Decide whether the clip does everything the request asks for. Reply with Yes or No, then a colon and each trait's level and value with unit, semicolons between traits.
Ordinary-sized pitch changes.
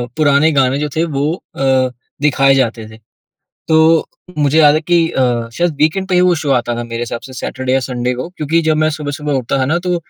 Yes: average, 3.7 semitones